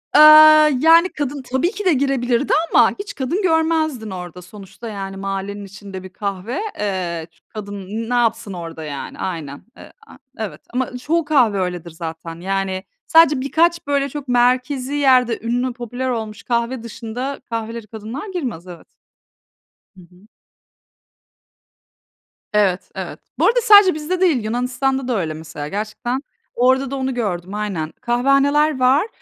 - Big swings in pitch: Yes, wide, 5.9 semitones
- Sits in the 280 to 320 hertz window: No, high, 240 Hz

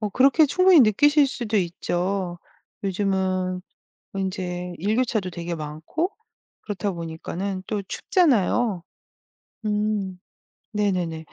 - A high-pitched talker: Yes, high, 195 Hz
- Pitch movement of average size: Yes, average, 3.5 semitones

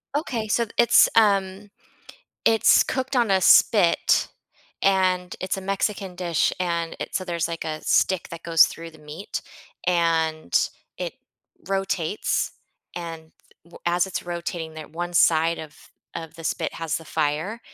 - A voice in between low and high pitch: Yes, medium, 175 Hz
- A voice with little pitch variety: No, average, 3.0 semitones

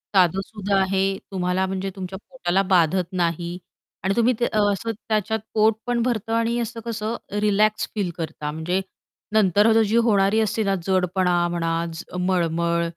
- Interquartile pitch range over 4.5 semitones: No, average, 3.3 semitones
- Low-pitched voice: No, high, 195 Hz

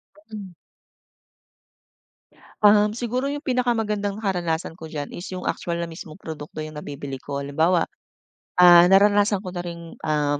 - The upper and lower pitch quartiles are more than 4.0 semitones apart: Yes, average, 4.7 semitones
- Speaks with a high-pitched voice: No, medium, 175 Hz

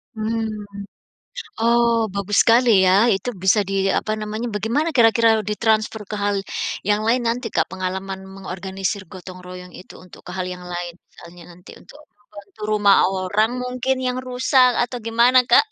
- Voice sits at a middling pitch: No, high, 210 Hz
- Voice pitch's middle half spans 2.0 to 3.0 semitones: No, average, 3.7 semitones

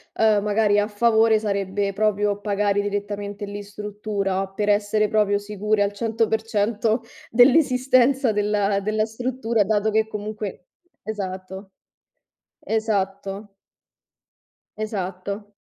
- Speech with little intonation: Yes, narrow, 1.4 semitones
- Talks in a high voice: Yes, high, 210 Hz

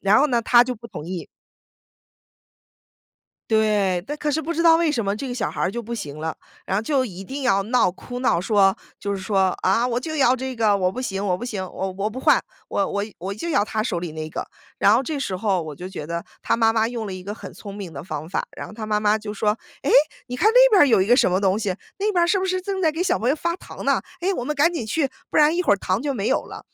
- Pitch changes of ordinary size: No, wide, 6.1 semitones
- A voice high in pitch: Yes, high, 220 Hz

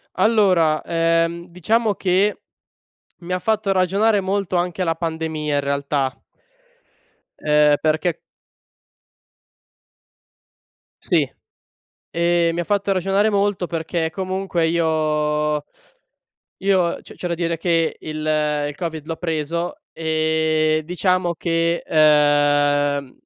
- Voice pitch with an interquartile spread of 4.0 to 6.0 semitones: No, average, 2.8 semitones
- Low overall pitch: No, medium, 165 Hz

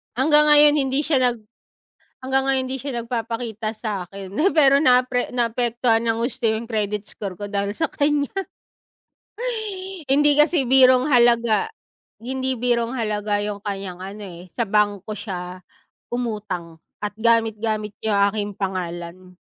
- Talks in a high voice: Yes, high, 230 Hz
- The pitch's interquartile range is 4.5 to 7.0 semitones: No, average, 4.0 semitones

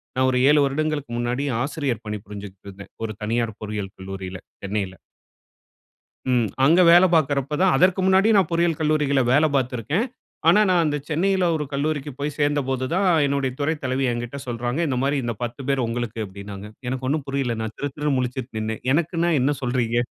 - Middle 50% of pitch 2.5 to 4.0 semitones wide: No, average, 4.6 semitones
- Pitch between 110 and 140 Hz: Yes, low, 135 Hz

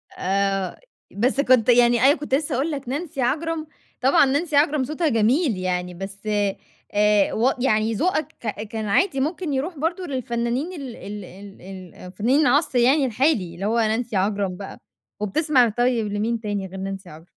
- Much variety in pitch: Yes, wide, 5.7 semitones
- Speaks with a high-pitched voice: Yes, high, 240 Hz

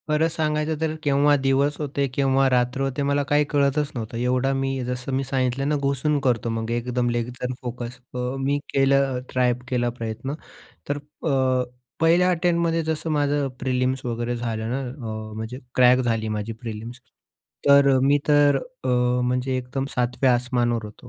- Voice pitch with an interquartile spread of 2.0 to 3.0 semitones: Yes, average, 2.7 semitones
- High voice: No, low, 130 Hz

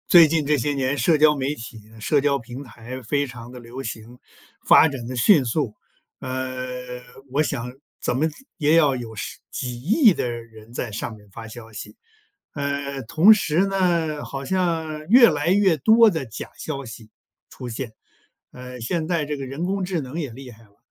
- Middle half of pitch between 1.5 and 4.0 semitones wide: No, average, 4.7 semitones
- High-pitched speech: No, low, 135 Hz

